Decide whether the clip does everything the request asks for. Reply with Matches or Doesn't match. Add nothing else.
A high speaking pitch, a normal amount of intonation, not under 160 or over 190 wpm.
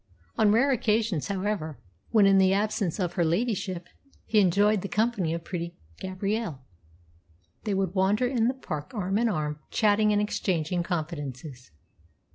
Doesn't match